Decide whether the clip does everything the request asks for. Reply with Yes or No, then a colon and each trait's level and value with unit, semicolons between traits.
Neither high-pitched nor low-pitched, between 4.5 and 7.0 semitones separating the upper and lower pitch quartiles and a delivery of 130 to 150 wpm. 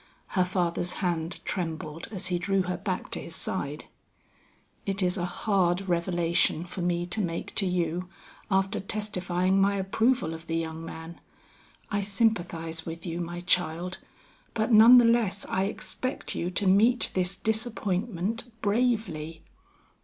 No: medium, 180 Hz; average, 2.9 semitones; average, 145 wpm